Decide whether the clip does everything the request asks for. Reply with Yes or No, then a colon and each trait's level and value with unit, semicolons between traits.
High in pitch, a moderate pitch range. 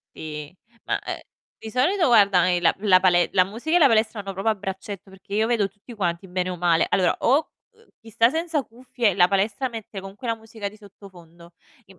Yes: high, 200 Hz; average, 3.8 semitones